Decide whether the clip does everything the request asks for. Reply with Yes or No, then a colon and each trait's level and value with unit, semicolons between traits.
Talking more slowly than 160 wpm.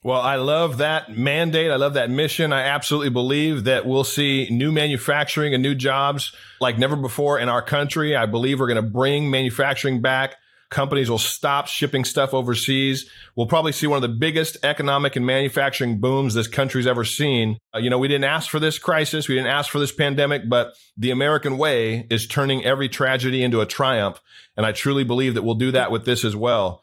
No: fast, 205 wpm